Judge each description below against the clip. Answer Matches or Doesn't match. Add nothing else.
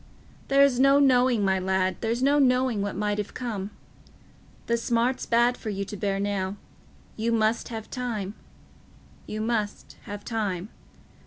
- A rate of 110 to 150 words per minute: Matches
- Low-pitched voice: Doesn't match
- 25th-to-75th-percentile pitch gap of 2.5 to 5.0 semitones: Matches